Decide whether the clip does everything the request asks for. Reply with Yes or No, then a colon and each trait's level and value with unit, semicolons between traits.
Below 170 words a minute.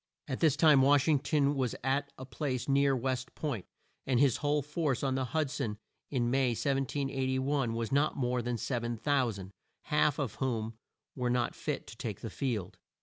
No: average, 180 wpm